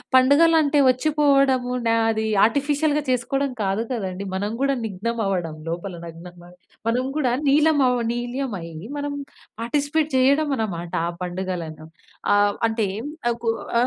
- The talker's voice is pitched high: Yes, high, 245 Hz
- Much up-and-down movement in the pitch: Yes, wide, 6.3 semitones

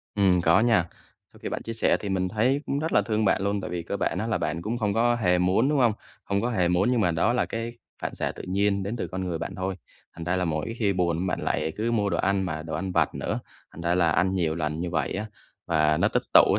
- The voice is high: No, very low, 95 Hz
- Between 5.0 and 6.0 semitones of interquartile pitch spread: No, average, 4.2 semitones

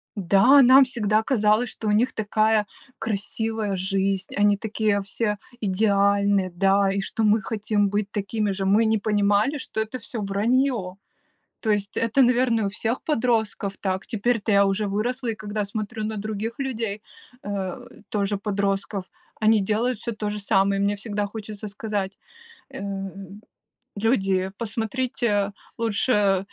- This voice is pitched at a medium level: No, high, 210 Hz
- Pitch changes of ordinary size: No, narrow, 2.0 semitones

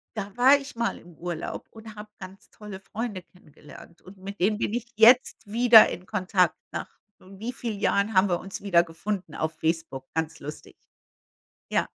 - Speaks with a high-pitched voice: Yes, high, 195 Hz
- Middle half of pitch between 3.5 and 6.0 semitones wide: Yes, average, 4.1 semitones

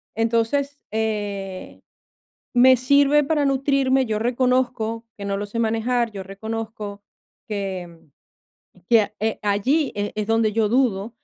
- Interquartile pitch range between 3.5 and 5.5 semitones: Yes, average, 3.8 semitones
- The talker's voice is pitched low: No, high, 225 Hz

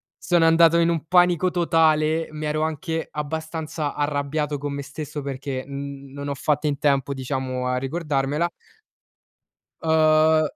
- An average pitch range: No, narrow, 2.3 semitones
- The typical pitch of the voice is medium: Yes, medium, 150 Hz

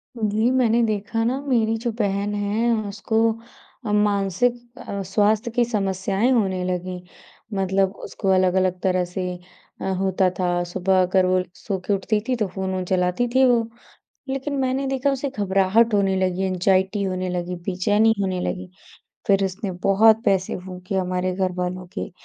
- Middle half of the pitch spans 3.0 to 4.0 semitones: Yes, average, 3.3 semitones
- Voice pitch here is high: Yes, high, 195 Hz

